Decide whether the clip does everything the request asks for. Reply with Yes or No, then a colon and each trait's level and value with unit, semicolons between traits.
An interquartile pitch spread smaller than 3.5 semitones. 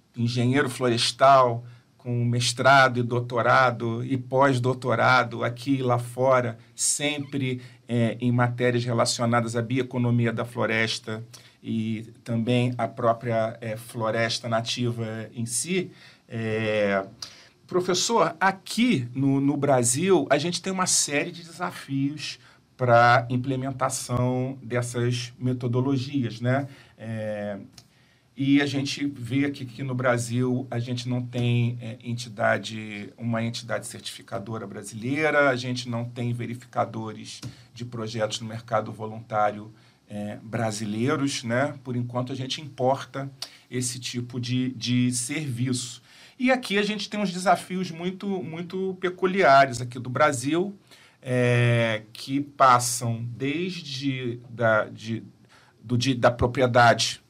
Yes: average, 2.8 semitones